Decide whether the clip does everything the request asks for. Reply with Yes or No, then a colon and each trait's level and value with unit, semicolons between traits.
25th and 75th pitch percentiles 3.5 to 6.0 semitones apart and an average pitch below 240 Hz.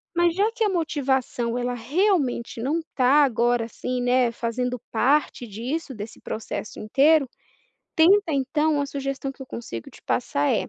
No: average, 4.4 semitones; very high, 265 Hz